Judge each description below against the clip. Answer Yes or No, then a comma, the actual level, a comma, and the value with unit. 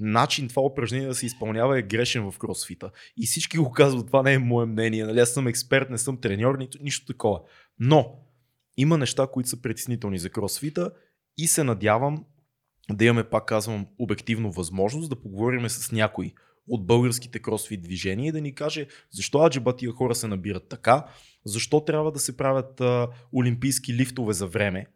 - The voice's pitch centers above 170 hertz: No, low, 125 Hz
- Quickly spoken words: Yes, fast, 175 wpm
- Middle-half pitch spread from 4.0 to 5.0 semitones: No, average, 3.6 semitones